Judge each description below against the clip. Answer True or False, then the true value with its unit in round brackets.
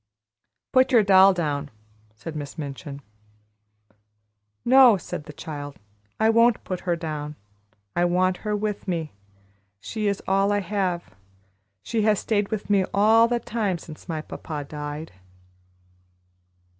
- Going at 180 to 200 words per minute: False (135 wpm)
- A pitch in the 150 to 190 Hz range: True (185 Hz)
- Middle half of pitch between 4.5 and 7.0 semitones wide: True (5.5 semitones)